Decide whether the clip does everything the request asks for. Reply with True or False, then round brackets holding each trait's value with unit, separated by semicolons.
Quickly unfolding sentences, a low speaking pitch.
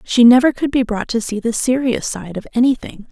False (230 wpm; 240 Hz)